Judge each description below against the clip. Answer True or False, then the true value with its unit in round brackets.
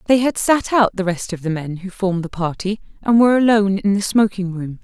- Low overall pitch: False (200 Hz)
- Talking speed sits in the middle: False (250 wpm)